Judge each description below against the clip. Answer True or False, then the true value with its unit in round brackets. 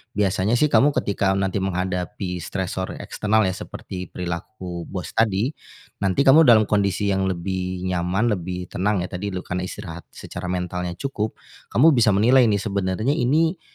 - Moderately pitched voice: False (95 Hz)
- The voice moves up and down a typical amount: True (3.1 semitones)